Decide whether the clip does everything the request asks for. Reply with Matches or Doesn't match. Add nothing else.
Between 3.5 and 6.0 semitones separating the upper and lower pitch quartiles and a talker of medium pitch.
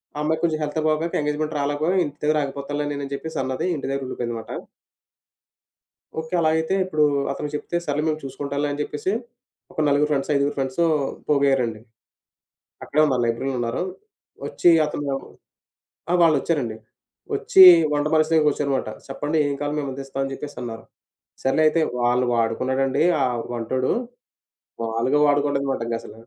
Doesn't match